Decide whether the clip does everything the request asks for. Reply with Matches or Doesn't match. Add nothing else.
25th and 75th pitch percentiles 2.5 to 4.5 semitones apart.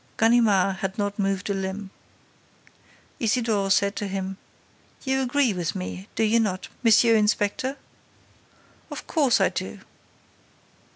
Matches